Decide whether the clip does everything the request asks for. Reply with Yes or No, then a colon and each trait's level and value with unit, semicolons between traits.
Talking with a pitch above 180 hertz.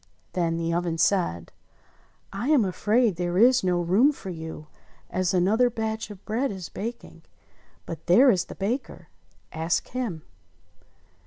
Yes: high, 190 Hz